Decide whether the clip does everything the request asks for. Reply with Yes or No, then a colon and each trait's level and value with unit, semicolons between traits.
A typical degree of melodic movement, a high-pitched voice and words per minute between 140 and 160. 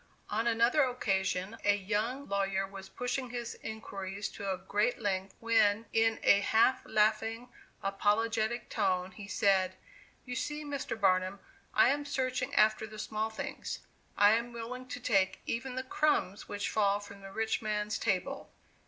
Yes: average, 3.2 semitones; high, 215 Hz; average, 155 wpm